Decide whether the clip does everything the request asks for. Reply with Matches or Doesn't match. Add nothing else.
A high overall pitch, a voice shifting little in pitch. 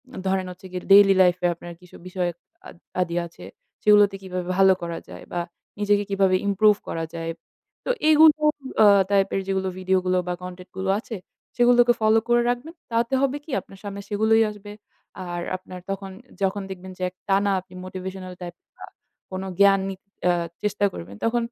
Matches